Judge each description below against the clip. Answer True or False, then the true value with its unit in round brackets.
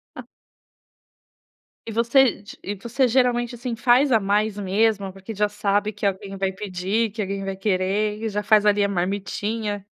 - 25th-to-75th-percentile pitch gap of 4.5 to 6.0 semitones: False (2.4 semitones)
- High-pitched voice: True (210 Hz)